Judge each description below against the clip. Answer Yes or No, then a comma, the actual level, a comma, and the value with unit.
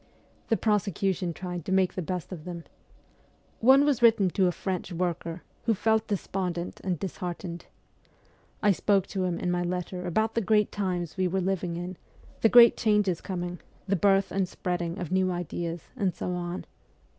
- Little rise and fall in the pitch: Yes, narrow, 2.2 semitones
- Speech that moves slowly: No, average, 175 wpm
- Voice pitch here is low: No, medium, 185 Hz